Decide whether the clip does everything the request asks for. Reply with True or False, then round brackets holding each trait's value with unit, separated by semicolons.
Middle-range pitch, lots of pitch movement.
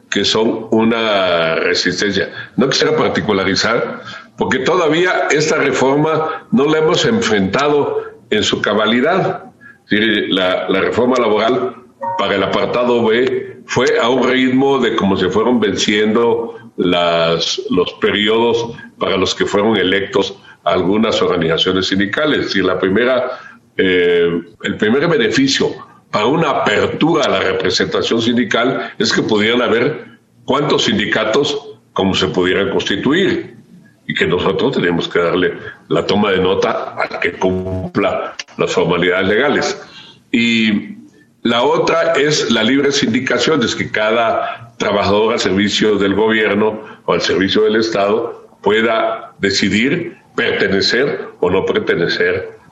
False (115 Hz; 6.4 semitones)